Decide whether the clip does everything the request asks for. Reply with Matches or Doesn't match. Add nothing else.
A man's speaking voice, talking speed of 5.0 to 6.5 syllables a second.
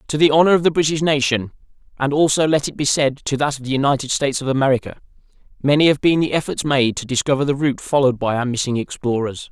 Doesn't match